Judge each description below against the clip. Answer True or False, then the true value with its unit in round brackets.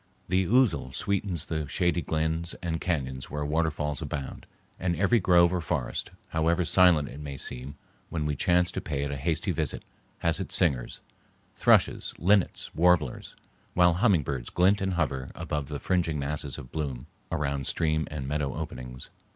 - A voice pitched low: True (80 Hz)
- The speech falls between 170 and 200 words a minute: False (155 wpm)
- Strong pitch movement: False (3.8 semitones)